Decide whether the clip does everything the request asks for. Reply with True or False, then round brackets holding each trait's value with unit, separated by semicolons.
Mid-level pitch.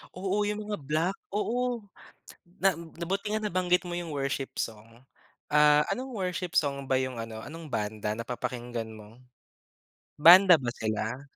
True (150 Hz)